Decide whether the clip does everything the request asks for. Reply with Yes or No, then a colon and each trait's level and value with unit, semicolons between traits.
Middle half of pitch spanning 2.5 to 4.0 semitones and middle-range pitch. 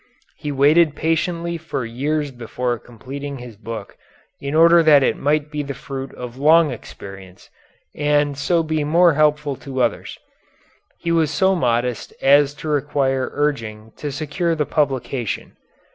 Yes: average, 3.3 semitones; medium, 145 Hz